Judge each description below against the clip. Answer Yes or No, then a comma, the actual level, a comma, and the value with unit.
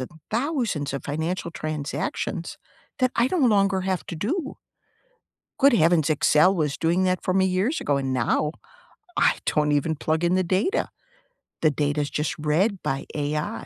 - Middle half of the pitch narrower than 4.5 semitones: No, average, 4.8 semitones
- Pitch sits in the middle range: Yes, medium, 170 Hz